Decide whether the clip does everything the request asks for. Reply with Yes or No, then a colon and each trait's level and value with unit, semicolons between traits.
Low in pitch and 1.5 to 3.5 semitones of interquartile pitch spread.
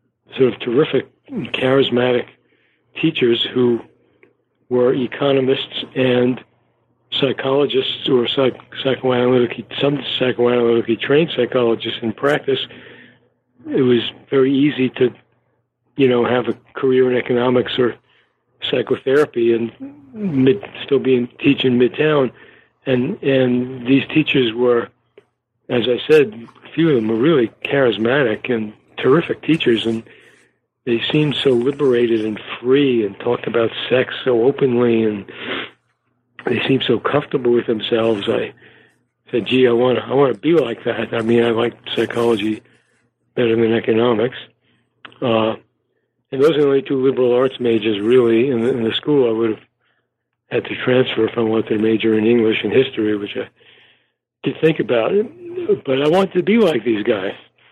Yes: low, 125 Hz; average, 2.7 semitones